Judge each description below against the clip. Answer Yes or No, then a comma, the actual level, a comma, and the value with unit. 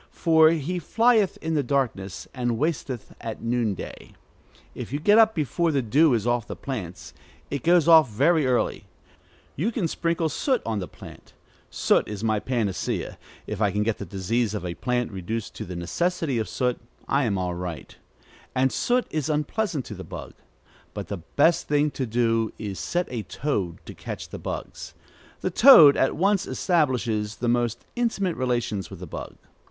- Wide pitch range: Yes, wide, 7.3 semitones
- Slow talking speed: No, average, 180 wpm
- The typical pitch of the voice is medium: No, low, 125 Hz